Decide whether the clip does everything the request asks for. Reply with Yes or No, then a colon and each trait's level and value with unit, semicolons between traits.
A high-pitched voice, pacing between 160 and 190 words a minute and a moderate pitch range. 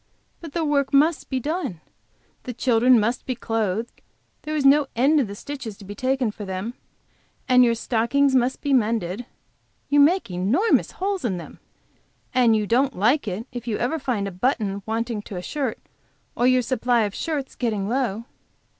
Yes: high, 245 Hz; average, 180 wpm; average, 4.3 semitones